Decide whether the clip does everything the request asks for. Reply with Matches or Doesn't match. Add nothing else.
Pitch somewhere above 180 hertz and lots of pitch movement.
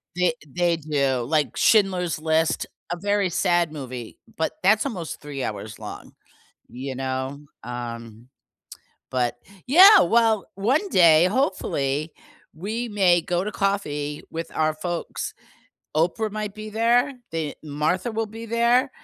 Doesn't match